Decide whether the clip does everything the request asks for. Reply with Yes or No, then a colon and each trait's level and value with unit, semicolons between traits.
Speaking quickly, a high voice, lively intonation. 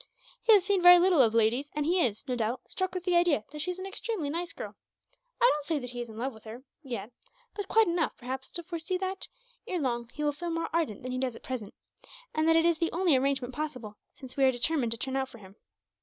Yes: fast, 260 wpm; very high, 290 Hz; wide, 5.9 semitones